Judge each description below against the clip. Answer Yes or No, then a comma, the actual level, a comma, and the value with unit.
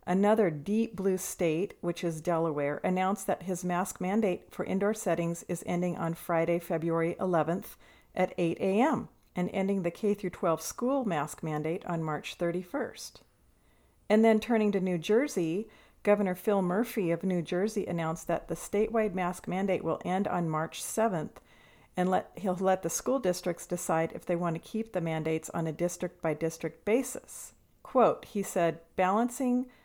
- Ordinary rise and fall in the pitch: Yes, average, 3.3 semitones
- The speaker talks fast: No, average, 160 wpm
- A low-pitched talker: No, medium, 180 Hz